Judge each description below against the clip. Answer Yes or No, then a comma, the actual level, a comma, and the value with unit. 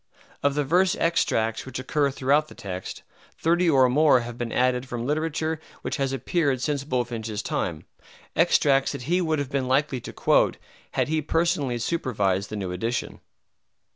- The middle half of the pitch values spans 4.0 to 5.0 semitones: Yes, average, 4.3 semitones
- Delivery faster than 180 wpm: No, average, 170 wpm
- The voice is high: No, low, 135 Hz